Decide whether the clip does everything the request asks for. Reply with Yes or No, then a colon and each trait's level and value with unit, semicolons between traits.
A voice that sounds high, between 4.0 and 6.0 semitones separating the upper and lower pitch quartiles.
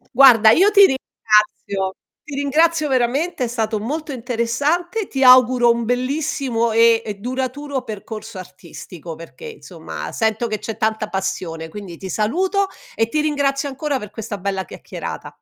Yes: high, 240 Hz; average, 4.9 semitones